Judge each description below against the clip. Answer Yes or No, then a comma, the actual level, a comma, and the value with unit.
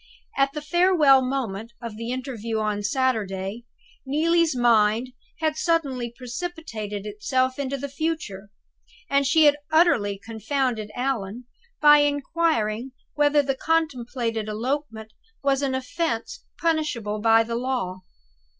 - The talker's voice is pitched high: Yes, very high, 255 Hz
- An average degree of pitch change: Yes, average, 4.9 semitones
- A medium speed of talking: No, slow, 120 wpm